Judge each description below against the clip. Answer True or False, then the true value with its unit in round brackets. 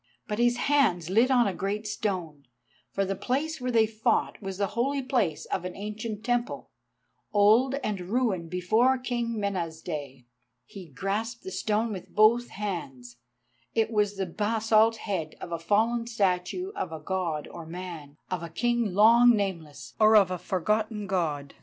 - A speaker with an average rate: True (170 wpm)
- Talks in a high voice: True (205 Hz)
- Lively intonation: False (4.5 semitones)